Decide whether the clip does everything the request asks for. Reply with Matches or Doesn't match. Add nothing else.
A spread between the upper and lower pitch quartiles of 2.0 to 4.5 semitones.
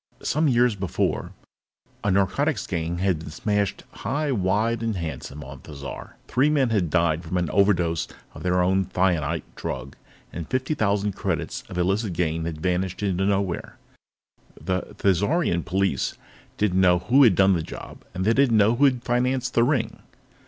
Doesn't match